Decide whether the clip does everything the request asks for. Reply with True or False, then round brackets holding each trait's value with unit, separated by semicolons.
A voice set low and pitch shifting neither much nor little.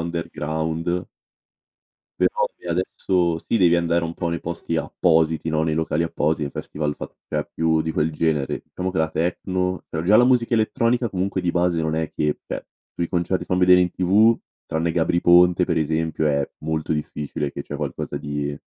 False (85 Hz; 2.3 semitones)